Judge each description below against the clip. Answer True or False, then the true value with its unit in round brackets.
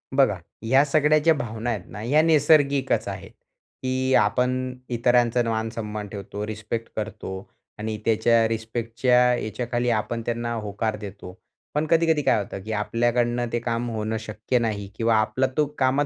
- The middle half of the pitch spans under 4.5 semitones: True (2.9 semitones)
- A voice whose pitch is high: False (115 Hz)